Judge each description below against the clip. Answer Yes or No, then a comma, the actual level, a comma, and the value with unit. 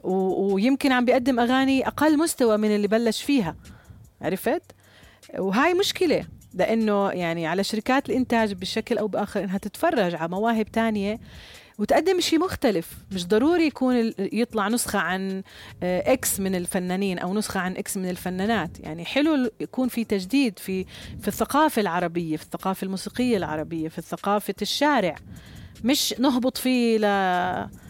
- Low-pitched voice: No, high, 210 Hz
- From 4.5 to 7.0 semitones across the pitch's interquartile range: Yes, average, 5.1 semitones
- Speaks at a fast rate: Yes, fast, 140 wpm